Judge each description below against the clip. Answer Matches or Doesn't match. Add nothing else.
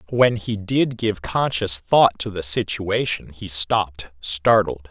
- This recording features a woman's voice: Doesn't match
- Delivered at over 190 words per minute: Doesn't match